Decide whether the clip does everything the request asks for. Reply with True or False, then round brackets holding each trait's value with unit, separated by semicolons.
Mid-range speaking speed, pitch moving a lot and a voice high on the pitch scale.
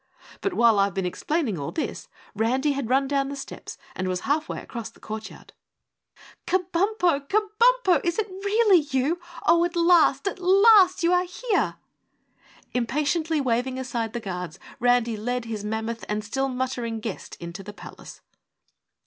True (155 wpm; 7.7 semitones; 270 Hz)